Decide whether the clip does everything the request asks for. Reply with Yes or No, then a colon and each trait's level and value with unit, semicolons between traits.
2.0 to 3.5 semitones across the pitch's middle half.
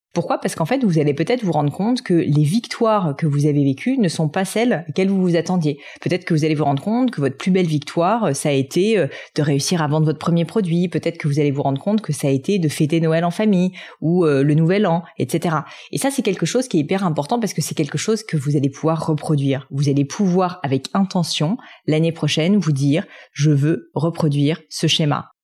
No: average, 4.2 semitones